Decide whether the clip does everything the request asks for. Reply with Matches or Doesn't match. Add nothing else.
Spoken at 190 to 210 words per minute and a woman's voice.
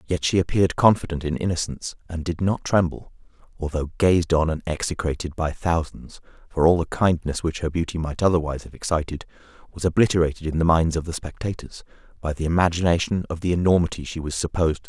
Doesn't match